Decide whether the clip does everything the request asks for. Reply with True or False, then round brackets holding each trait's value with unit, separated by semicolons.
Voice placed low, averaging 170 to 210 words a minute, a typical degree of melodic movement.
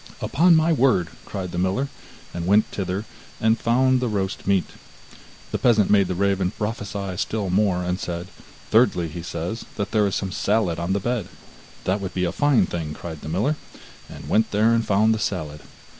True (100 Hz; 190 wpm; 3.7 semitones)